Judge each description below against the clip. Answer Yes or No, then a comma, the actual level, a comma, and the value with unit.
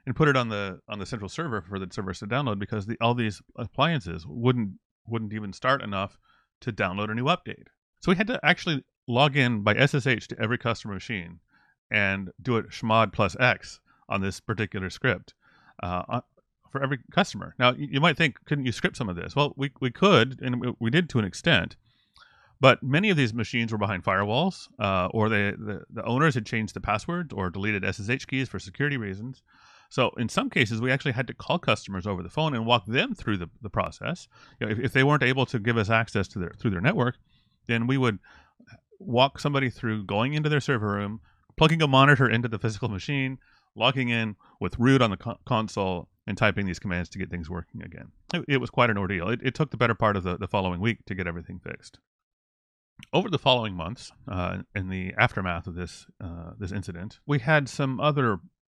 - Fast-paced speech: Yes, fast, 215 wpm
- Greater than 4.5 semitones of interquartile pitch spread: Yes, average, 5.0 semitones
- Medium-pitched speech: No, low, 115 Hz